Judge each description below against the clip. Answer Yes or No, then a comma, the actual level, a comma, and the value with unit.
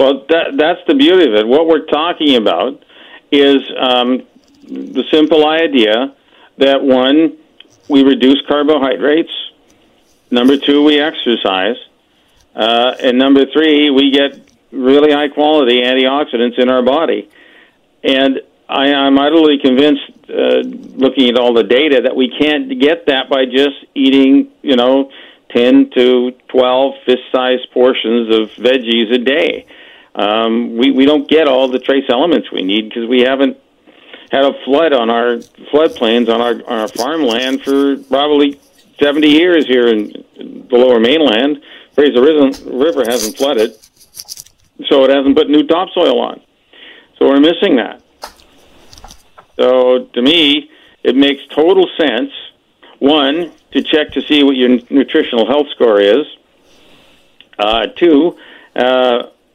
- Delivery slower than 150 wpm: Yes, average, 140 wpm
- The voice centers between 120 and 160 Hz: Yes, low, 135 Hz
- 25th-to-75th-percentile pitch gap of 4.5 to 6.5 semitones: No, average, 2.8 semitones